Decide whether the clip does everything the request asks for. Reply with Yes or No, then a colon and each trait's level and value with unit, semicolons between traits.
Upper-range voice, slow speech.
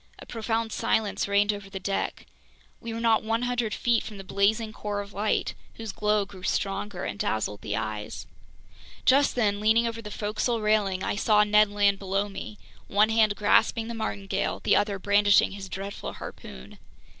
No: high, 210 Hz; average, 175 wpm